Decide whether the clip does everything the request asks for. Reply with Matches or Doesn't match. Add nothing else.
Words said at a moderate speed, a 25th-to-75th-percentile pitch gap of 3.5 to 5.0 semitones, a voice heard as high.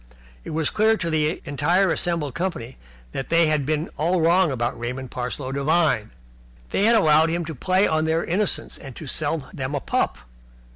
Doesn't match